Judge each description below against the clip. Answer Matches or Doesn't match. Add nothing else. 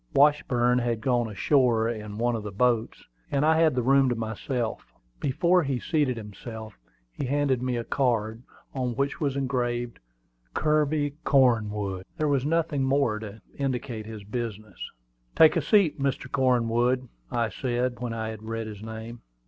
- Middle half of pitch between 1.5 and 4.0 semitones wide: Matches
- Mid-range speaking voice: Doesn't match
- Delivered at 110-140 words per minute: Doesn't match